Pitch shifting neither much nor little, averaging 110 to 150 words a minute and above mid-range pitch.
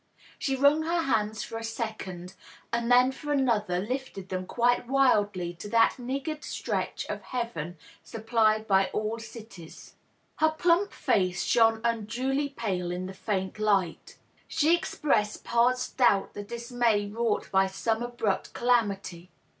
Yes: average, 4.0 semitones; average, 140 wpm; high, 225 Hz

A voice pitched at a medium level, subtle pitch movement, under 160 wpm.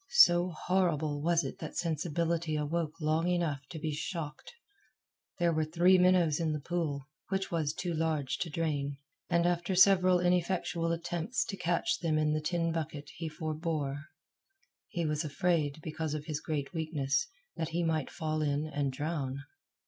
No: medium, 160 Hz; narrow, 2.3 semitones; average, 165 wpm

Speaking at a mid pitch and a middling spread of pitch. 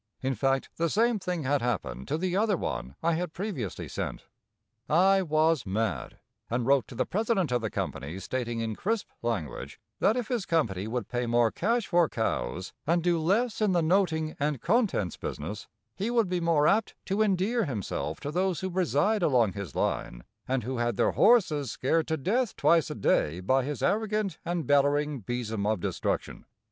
No: medium, 155 Hz; wide, 8.2 semitones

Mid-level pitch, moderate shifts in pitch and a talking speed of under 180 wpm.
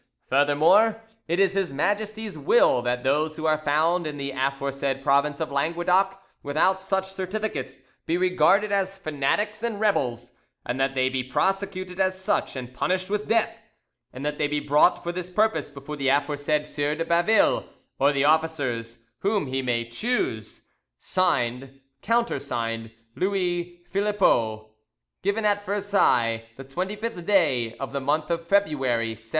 No: medium, 155 Hz; wide, 6.0 semitones; average, 150 wpm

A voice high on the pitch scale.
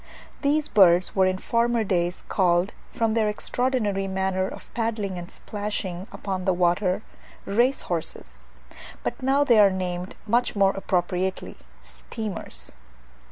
Yes: high, 195 Hz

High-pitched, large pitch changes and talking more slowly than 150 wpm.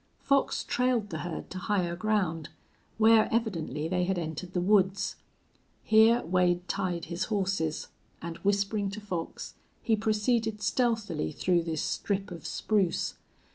No: high, 195 Hz; average, 3.9 semitones; slow, 135 wpm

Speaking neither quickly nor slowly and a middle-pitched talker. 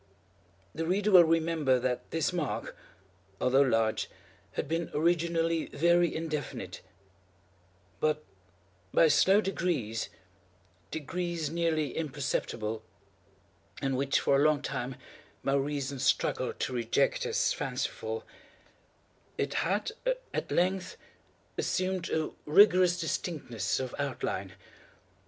No: slow, 100 wpm; medium, 155 Hz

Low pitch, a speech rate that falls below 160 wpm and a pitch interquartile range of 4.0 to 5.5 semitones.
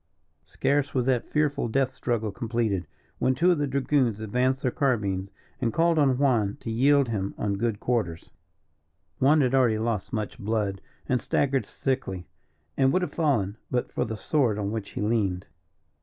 No: low, 120 Hz; average, 170 wpm; average, 4.4 semitones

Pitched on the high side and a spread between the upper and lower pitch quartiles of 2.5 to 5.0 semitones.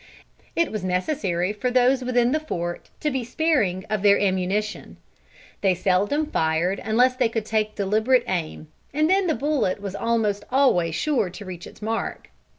No: high, 215 Hz; wide, 5.5 semitones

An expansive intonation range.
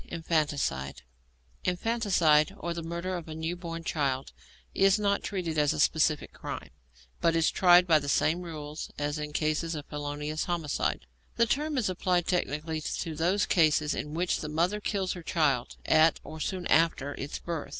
No: average, 3.0 semitones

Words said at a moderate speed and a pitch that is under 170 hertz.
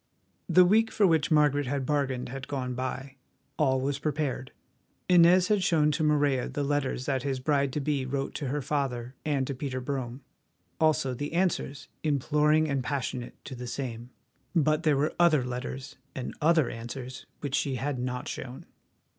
Yes: average, 170 wpm; medium, 140 Hz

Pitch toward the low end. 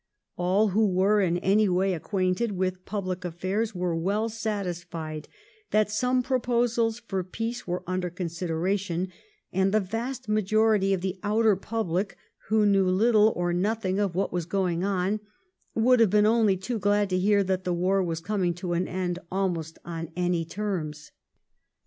No: high, 190 Hz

